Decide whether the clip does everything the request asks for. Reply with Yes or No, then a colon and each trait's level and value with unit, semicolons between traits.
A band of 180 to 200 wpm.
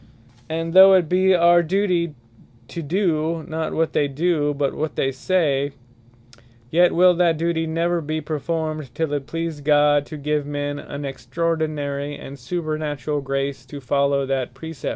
No: average, 155 wpm